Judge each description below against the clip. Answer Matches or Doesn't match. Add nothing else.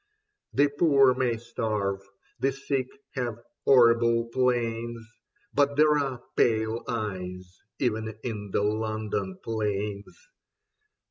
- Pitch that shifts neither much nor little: Matches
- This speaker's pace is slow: Matches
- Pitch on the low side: Matches